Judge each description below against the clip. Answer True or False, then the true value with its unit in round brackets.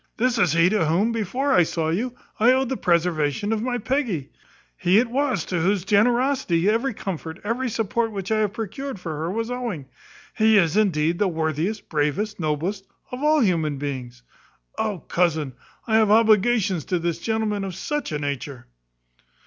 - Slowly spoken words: False (175 wpm)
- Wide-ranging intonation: True (5.7 semitones)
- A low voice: False (200 Hz)